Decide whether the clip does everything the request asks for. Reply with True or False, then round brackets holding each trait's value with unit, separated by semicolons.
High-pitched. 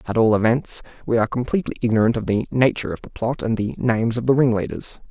False (115 Hz)